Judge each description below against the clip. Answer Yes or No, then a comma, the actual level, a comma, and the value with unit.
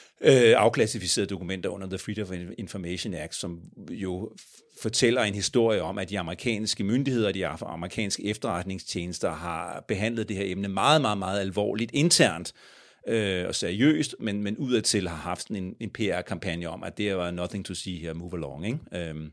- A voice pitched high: No, low, 100 Hz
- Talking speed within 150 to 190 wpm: Yes, average, 170 wpm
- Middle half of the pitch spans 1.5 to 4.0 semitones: Yes, average, 3.5 semitones